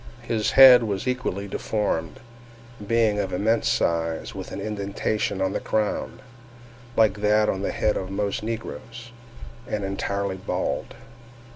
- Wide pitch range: No, narrow, 2.4 semitones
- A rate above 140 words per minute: No, slow, 135 wpm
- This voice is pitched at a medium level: No, low, 105 Hz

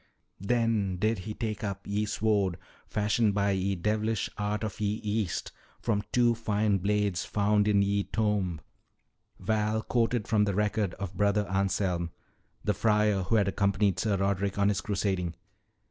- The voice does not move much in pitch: Yes, narrow, 1.4 semitones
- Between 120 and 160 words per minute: Yes, average, 155 wpm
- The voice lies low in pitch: Yes, low, 105 Hz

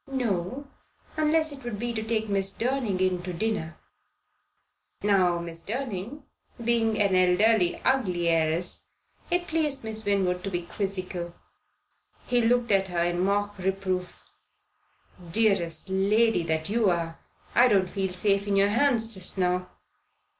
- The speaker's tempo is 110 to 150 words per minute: Yes, average, 140 wpm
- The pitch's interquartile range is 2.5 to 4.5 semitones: Yes, average, 4.1 semitones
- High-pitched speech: Yes, high, 200 Hz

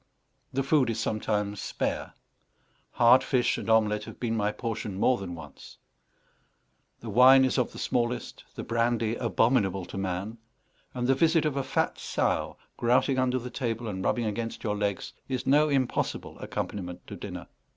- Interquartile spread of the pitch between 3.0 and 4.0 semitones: Yes, average, 3.6 semitones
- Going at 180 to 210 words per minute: No, average, 165 wpm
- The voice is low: Yes, low, 115 Hz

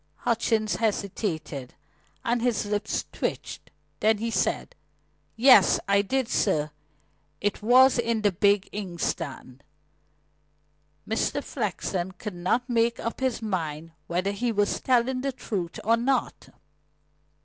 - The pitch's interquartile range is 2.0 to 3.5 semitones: No, average, 3.9 semitones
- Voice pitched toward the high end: Yes, high, 215 Hz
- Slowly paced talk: Yes, slow, 120 wpm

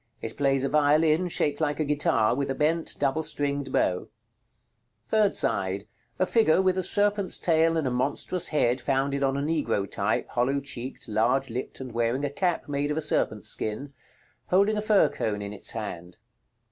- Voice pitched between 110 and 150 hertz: Yes, medium, 140 Hz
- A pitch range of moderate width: Yes, average, 4.7 semitones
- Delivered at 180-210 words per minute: Yes, average, 185 wpm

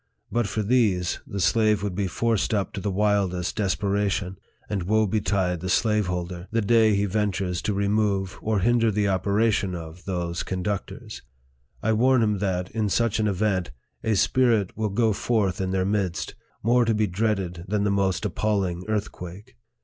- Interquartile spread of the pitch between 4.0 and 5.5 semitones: No, narrow, 2.6 semitones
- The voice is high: No, low, 100 Hz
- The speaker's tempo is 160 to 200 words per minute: Yes, average, 170 wpm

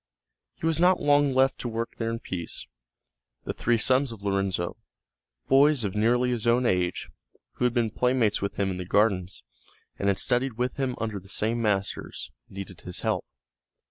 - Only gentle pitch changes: No, average, 4.3 semitones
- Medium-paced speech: Yes, average, 180 wpm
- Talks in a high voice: No, low, 115 Hz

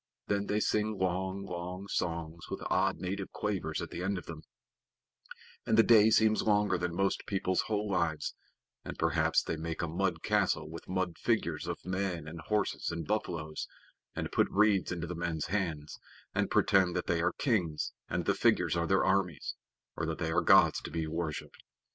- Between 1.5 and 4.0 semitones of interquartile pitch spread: Yes, average, 3.1 semitones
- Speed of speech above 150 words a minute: Yes, average, 185 wpm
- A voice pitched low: Yes, very low, 90 Hz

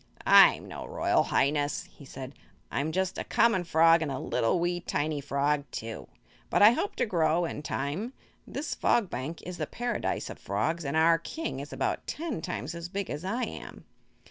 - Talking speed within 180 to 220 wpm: Yes, average, 190 wpm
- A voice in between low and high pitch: Yes, medium, 165 Hz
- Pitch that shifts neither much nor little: Yes, average, 4.8 semitones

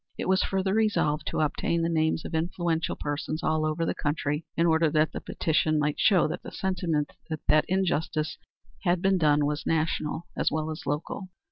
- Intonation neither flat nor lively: No, narrow, 2.3 semitones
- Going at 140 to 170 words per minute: No, average, 190 wpm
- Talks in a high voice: No, medium, 160 Hz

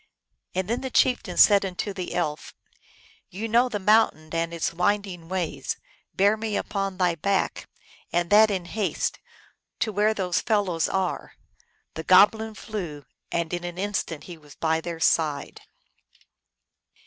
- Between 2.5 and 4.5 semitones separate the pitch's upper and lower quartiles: Yes, average, 3.6 semitones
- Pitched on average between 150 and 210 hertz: Yes, high, 190 Hz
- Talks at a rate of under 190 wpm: Yes, average, 160 wpm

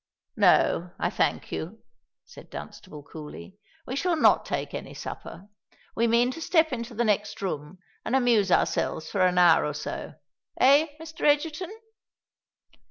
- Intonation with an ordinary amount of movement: No, wide, 8.0 semitones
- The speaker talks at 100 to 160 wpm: Yes, average, 145 wpm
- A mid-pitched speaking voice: No, high, 230 Hz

